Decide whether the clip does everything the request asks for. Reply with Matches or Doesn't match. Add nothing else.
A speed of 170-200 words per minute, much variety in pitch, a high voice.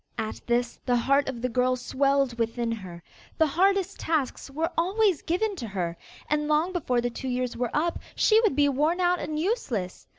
Matches